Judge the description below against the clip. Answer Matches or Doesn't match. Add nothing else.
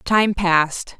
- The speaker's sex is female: Matches